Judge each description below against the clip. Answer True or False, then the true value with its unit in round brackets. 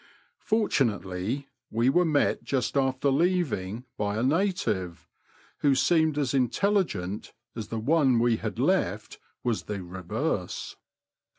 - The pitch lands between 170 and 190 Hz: False (130 Hz)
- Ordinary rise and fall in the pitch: False (6.6 semitones)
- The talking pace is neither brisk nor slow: False (120 wpm)